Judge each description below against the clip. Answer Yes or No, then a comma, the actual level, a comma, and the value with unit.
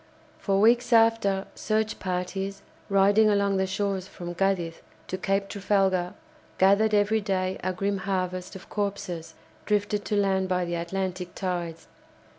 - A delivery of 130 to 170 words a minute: Yes, average, 140 wpm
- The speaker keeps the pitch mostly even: Yes, narrow, 1.7 semitones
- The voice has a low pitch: No, high, 195 Hz